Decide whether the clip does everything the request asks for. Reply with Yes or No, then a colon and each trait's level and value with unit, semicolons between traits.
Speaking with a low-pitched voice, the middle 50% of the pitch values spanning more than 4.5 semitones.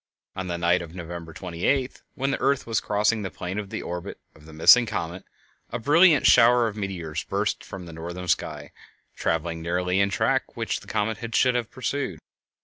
Yes: very low, 95 Hz; average, 5.2 semitones